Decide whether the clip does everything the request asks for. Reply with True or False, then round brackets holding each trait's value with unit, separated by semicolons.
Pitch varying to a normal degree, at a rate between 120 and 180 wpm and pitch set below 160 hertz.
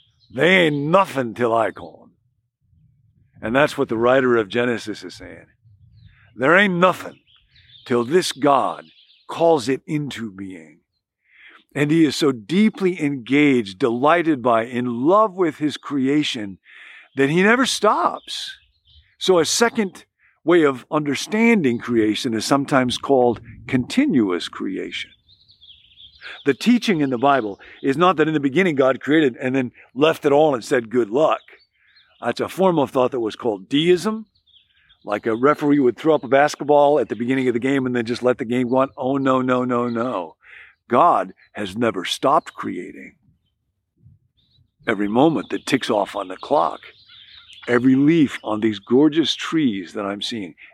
True (4.7 semitones; 160 wpm; 135 Hz)